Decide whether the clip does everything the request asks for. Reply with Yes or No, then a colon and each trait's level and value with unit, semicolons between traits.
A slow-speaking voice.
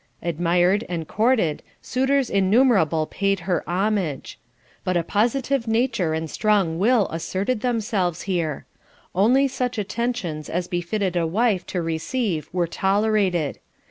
Yes: slow, 125 wpm